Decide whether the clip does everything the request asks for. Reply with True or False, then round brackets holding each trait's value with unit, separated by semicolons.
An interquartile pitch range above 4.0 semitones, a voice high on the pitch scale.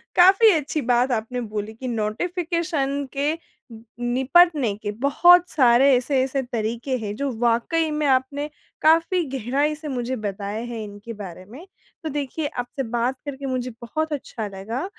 True (4.5 semitones; 260 Hz)